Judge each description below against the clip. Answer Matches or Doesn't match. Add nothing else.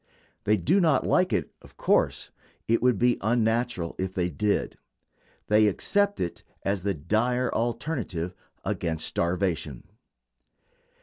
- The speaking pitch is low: Matches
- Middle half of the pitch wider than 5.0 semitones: Matches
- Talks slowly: Matches